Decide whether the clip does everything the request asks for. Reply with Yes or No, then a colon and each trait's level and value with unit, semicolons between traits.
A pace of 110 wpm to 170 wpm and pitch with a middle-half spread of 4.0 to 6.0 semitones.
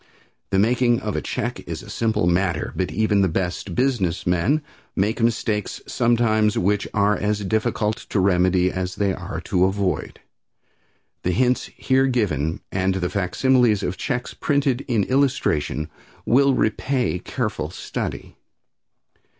Yes: average, 140 wpm; average, 4.6 semitones